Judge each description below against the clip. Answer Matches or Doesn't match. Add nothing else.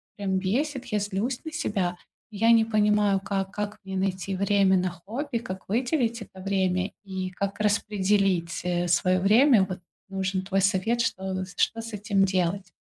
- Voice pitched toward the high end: Matches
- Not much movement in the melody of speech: Matches